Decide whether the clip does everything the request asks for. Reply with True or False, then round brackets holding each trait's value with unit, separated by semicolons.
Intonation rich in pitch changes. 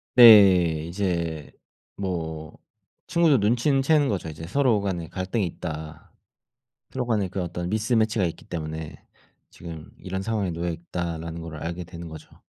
False (4.4 semitones)